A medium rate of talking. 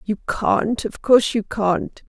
Yes: average, 170 wpm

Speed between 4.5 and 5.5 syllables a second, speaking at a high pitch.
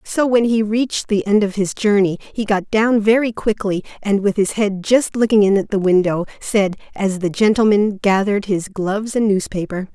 Yes: 5.0 syllables/s; high, 205 Hz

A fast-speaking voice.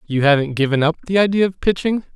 Yes: fast, 225 wpm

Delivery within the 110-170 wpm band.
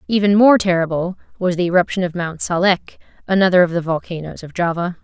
No: average, 180 wpm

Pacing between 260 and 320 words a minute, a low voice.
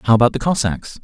No: fast, 235 wpm; low, 120 Hz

